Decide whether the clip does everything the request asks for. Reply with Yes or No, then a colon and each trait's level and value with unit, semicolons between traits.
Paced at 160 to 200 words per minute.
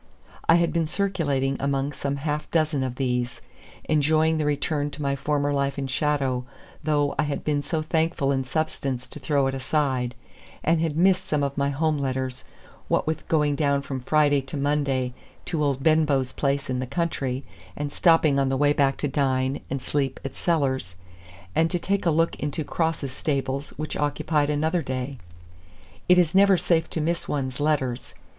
Yes: average, 180 wpm